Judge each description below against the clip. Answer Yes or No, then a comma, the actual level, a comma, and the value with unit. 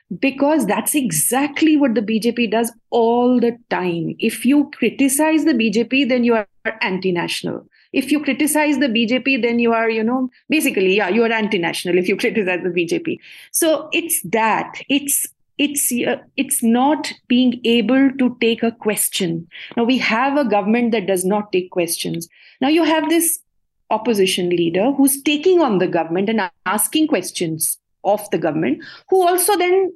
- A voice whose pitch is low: No, high, 235 Hz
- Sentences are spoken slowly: No, average, 170 wpm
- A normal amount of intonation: No, wide, 5.7 semitones